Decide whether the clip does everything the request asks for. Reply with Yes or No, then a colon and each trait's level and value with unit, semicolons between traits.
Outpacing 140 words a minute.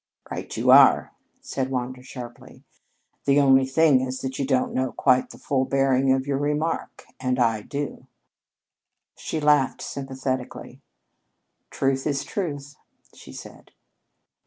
No: slow, 135 wpm